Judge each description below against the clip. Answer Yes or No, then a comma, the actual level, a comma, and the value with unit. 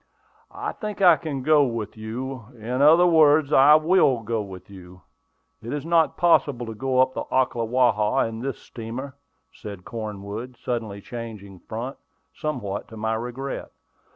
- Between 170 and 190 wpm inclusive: No, average, 155 wpm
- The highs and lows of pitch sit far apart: No, average, 4.4 semitones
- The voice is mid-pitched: No, low, 120 Hz